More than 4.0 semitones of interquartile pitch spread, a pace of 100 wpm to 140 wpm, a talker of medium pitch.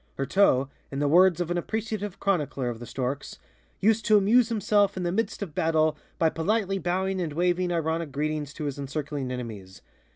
No: wide, 5.4 semitones; average, 185 wpm; medium, 165 Hz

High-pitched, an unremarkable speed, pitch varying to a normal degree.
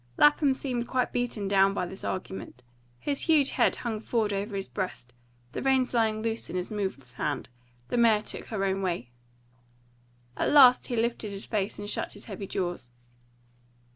Yes: high, 210 Hz; average, 175 wpm; average, 4.0 semitones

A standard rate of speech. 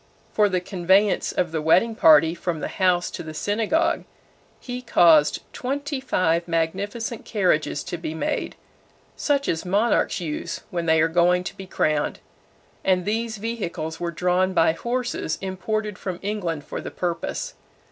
Yes: average, 155 wpm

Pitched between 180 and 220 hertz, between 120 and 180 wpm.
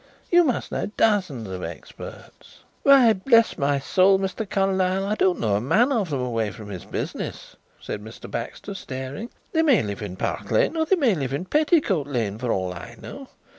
No: medium, 185 Hz; average, 195 wpm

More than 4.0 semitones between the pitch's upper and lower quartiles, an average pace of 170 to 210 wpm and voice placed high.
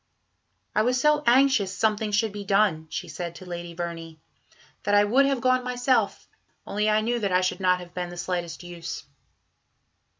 Yes: average, 5.2 semitones; average, 180 wpm; high, 205 Hz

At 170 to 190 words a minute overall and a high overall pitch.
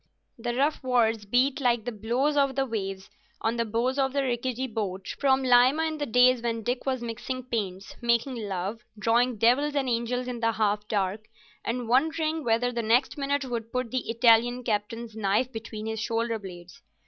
Yes: average, 185 wpm; high, 235 Hz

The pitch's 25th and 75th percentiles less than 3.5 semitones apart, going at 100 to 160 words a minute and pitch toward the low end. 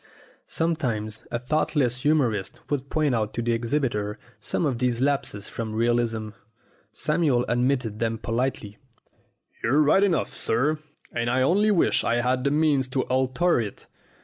No: average, 4.1 semitones; average, 150 wpm; low, 125 Hz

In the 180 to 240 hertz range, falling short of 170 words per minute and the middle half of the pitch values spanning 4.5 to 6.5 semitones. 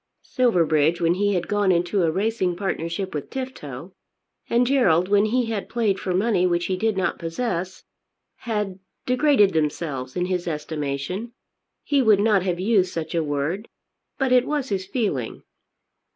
Yes: high, 190 Hz; average, 160 wpm; average, 4.8 semitones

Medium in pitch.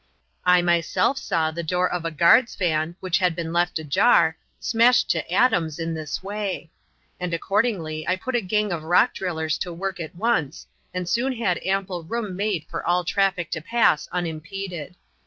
Yes: medium, 180 Hz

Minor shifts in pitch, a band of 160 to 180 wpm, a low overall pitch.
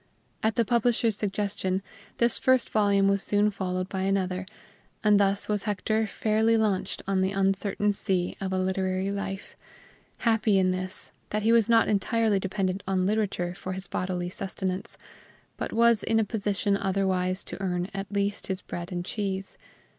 No: narrow, 2.0 semitones; average, 165 wpm; high, 195 Hz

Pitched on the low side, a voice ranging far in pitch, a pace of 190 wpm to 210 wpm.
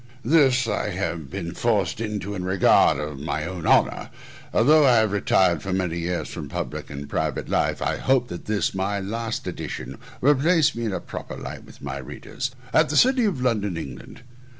Yes: low, 100 Hz; wide, 6.4 semitones; average, 195 wpm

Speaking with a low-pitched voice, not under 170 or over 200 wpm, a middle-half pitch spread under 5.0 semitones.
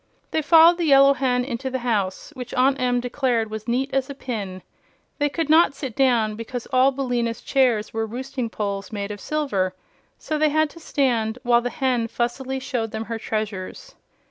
No: very high, 250 Hz; average, 190 wpm; average, 3.5 semitones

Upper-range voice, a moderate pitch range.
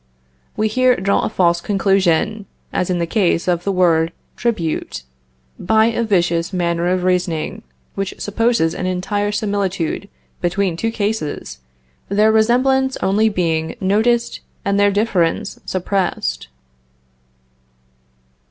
Yes: high, 195 Hz; average, 3.8 semitones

